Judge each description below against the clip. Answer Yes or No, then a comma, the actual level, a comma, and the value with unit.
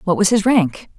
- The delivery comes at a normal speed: No, fast, 245 wpm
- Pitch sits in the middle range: No, high, 195 Hz